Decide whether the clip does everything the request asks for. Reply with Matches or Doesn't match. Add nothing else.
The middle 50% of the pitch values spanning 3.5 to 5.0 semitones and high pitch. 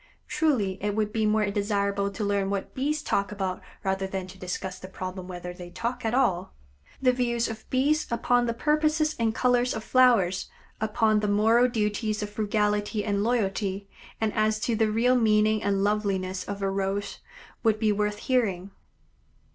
Doesn't match